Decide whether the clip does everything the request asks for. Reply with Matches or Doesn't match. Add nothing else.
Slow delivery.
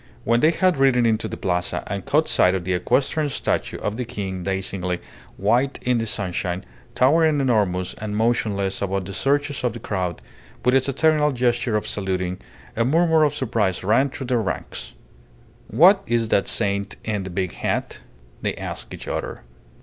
Doesn't match